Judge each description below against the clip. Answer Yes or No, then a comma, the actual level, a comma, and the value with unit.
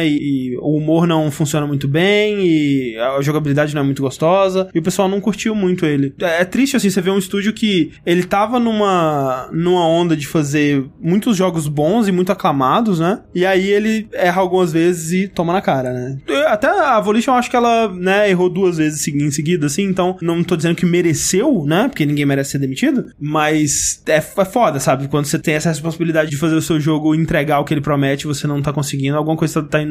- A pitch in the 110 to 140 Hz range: No, medium, 165 Hz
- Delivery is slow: No, fast, 220 wpm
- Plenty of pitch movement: No, average, 4.3 semitones